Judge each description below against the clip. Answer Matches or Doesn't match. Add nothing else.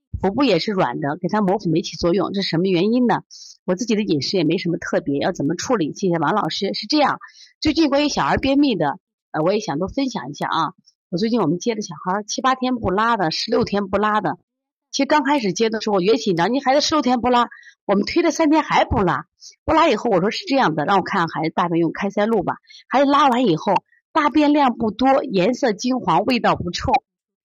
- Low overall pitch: Doesn't match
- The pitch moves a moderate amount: Doesn't match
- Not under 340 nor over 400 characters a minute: Matches